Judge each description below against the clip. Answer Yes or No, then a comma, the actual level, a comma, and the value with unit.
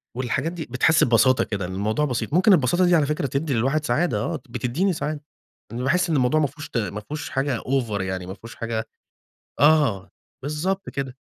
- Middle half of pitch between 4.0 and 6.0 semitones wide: Yes, average, 5.1 semitones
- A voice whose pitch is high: No, low, 135 Hz